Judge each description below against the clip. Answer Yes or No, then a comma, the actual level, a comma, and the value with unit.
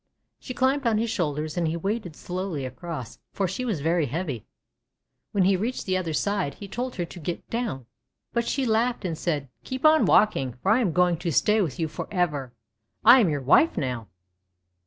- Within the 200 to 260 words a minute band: Yes, fast, 205 wpm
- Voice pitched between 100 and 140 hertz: No, medium, 180 Hz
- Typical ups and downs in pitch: No, wide, 6.3 semitones